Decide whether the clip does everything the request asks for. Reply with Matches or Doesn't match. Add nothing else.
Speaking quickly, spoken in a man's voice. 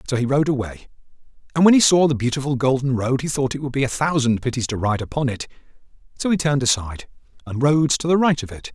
Matches